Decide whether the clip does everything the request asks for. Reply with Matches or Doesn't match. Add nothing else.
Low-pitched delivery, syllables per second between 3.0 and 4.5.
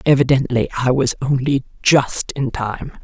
Matches